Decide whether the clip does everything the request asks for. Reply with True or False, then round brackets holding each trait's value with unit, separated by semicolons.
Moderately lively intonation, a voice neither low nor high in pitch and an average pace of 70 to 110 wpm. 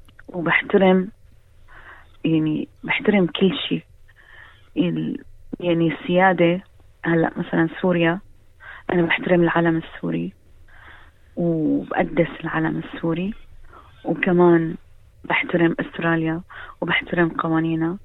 False (1.8 semitones; 170 Hz; 75 wpm)